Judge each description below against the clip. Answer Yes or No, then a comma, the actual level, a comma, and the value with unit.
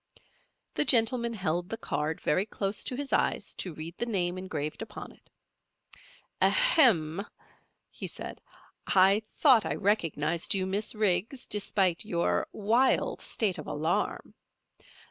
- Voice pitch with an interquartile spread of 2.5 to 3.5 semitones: No, average, 4.6 semitones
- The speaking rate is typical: No, slow, 130 wpm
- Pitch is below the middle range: No, high, 195 Hz